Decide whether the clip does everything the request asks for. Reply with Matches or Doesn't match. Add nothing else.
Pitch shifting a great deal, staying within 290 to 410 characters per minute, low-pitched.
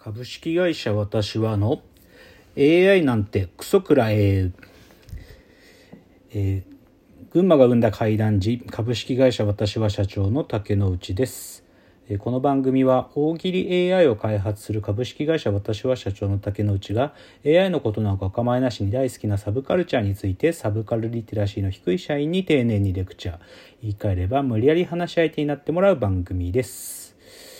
Doesn't match